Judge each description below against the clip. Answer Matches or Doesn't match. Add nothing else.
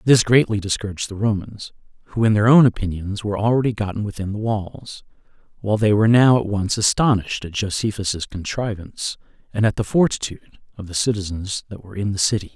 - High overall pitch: Doesn't match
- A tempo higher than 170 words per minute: Matches